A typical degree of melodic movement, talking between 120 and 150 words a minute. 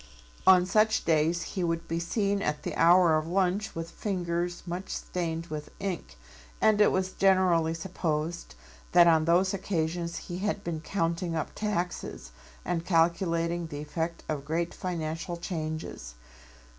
No: narrow, 2.2 semitones; average, 145 wpm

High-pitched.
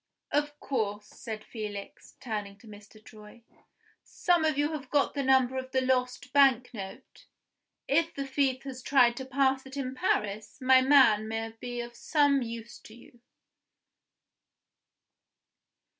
Yes: very high, 255 Hz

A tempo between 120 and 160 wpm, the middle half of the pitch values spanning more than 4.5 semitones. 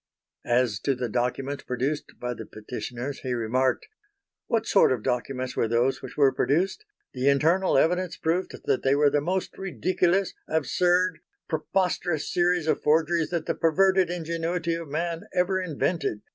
Yes: average, 155 wpm; average, 5.3 semitones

